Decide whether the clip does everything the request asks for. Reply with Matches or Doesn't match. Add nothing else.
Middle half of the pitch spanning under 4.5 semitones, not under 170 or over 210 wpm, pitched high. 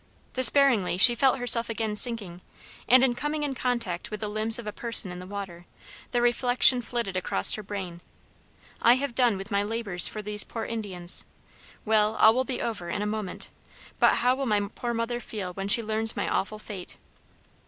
Matches